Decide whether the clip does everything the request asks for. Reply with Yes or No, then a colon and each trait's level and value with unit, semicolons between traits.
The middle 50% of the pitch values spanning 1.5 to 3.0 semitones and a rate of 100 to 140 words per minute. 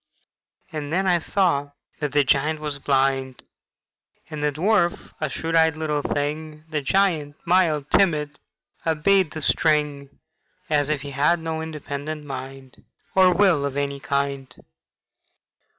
Yes: narrow, 2.5 semitones; slow, 135 wpm